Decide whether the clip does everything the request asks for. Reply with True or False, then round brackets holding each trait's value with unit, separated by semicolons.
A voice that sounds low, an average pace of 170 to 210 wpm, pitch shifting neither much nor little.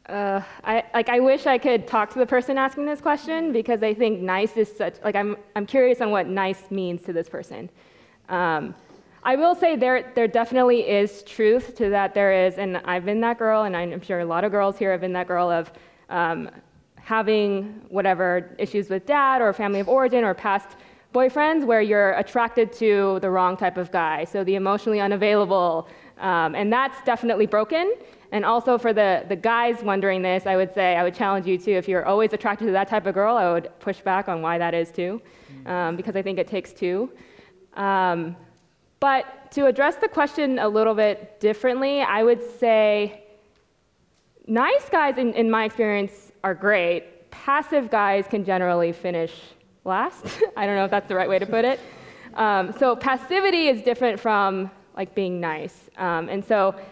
False (205 Hz; 195 wpm; 3.8 semitones)